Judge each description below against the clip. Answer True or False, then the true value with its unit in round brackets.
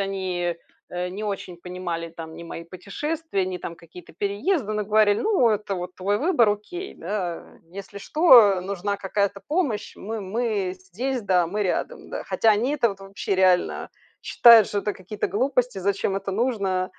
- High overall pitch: True (200 Hz)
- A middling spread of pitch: True (3.1 semitones)